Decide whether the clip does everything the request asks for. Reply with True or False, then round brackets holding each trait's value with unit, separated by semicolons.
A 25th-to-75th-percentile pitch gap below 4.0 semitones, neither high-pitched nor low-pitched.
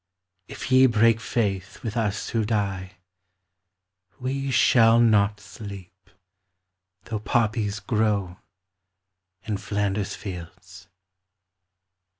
False (2.6 semitones; 105 Hz)